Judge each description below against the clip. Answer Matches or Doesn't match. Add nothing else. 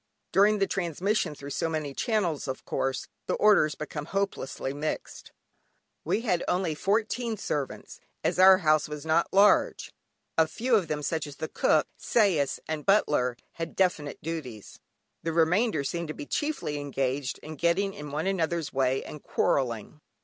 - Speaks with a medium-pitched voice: Matches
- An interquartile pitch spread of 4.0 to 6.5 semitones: Matches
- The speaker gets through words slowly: Doesn't match